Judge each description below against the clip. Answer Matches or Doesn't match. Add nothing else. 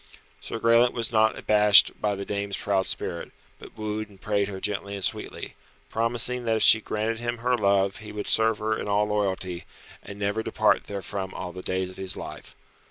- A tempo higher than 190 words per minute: Matches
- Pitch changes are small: Matches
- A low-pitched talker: Matches